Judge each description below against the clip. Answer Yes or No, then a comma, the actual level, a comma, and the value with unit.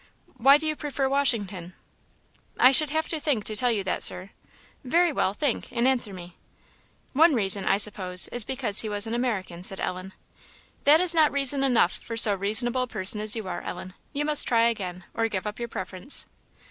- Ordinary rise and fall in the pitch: No, wide, 5.8 semitones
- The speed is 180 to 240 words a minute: Yes, average, 200 wpm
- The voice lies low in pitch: No, high, 230 Hz